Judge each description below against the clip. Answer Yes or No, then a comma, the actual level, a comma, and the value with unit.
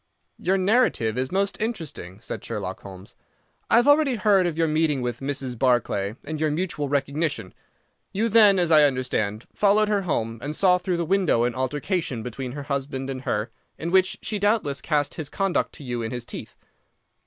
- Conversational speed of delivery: Yes, average, 190 wpm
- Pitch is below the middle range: No, medium, 145 Hz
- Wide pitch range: Yes, wide, 7.2 semitones